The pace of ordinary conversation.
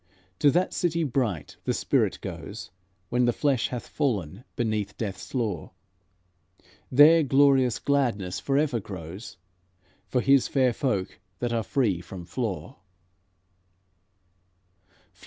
No: slow, 115 wpm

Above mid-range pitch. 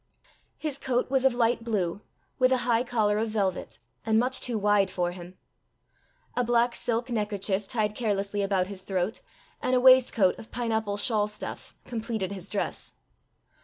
Yes: high, 220 Hz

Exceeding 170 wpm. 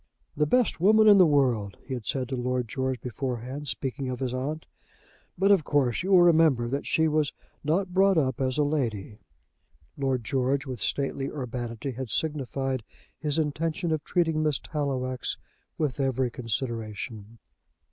No: average, 160 wpm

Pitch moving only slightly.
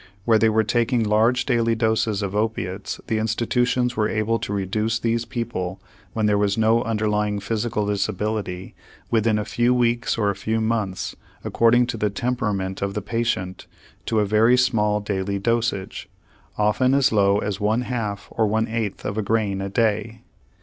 Yes: narrow, 2.2 semitones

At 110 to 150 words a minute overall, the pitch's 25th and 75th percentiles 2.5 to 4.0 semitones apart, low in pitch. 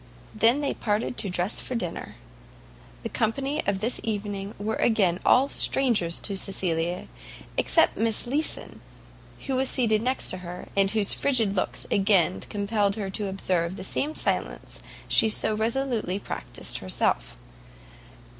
No: average, 145 wpm; average, 3.5 semitones; high, 210 Hz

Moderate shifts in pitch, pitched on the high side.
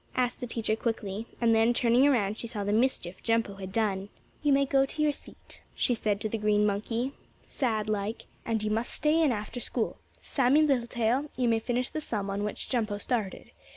Yes: average, 3.1 semitones; high, 230 Hz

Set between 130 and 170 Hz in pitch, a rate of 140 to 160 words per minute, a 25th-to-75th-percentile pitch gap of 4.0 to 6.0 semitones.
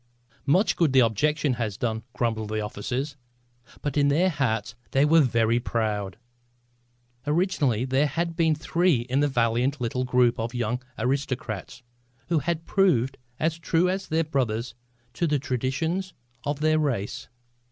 Yes: low, 135 Hz; average, 150 wpm; average, 5.0 semitones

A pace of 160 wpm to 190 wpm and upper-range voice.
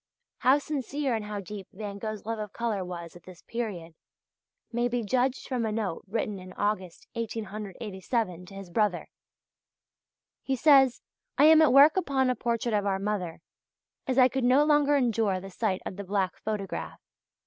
Yes: average, 175 wpm; high, 215 Hz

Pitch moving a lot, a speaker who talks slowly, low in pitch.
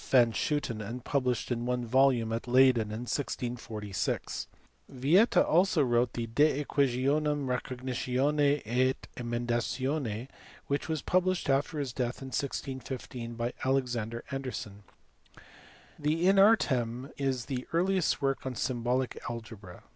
No: average, 3.0 semitones; slow, 125 wpm; low, 130 Hz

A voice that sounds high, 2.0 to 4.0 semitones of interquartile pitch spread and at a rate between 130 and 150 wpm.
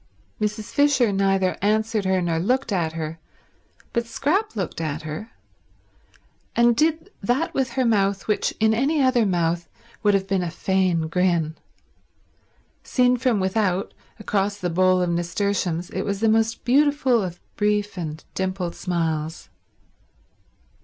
No: high, 195 Hz; average, 4.7 semitones; average, 140 wpm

